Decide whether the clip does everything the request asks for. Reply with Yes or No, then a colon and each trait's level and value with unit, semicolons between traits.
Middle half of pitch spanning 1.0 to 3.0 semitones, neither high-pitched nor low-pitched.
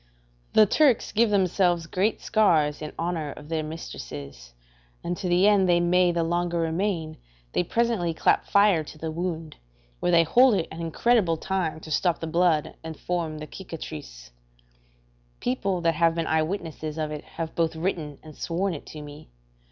Yes: average, 2.7 semitones; medium, 165 Hz